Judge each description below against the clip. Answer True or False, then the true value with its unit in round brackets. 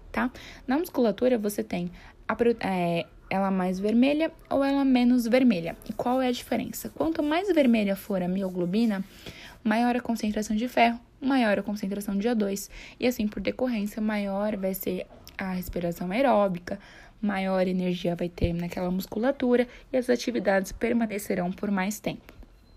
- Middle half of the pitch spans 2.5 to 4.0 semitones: False (4.5 semitones)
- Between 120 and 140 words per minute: False (155 wpm)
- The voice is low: False (215 Hz)